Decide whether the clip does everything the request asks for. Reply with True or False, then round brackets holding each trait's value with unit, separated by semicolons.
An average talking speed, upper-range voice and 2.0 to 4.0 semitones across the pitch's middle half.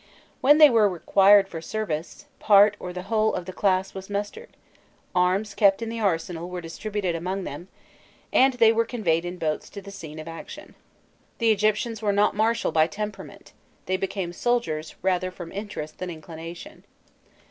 True (170 wpm; 195 Hz; 3.6 semitones)